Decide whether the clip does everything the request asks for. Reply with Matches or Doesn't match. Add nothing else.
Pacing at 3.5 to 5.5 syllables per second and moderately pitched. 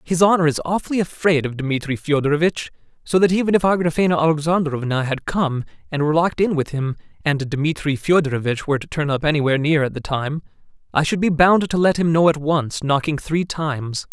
Doesn't match